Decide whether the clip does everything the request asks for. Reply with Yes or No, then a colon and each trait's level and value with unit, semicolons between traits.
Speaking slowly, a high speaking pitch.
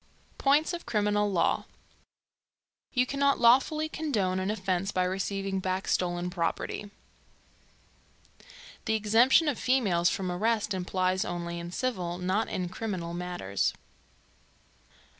Yes: slow, 115 wpm; high, 195 Hz